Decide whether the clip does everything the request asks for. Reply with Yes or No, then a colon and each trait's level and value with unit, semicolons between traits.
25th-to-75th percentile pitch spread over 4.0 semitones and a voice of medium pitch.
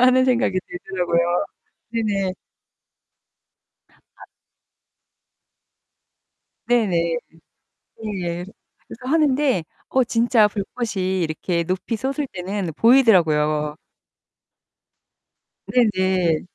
No: wide, 5.6 semitones; high, 195 Hz